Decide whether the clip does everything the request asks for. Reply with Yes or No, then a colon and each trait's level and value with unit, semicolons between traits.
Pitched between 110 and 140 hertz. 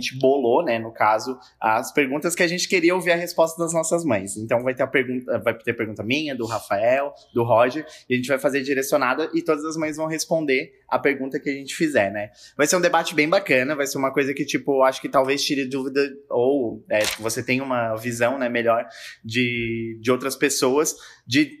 Yes: low, 135 Hz